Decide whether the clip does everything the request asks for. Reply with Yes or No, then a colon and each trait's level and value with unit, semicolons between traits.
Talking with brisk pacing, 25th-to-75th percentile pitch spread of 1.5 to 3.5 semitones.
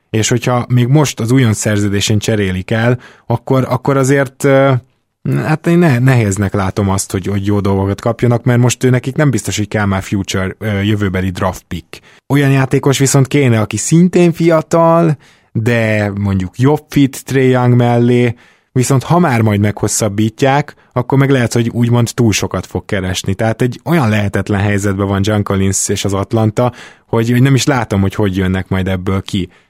No: fast, 175 wpm; average, 4.6 semitones